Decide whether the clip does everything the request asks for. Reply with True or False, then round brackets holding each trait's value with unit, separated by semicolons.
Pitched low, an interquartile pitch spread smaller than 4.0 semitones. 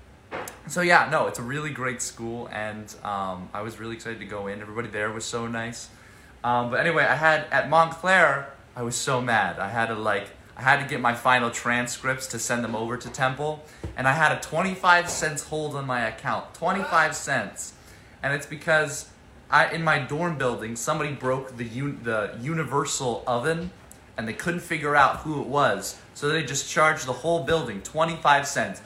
False (130 Hz; 4.7 semitones)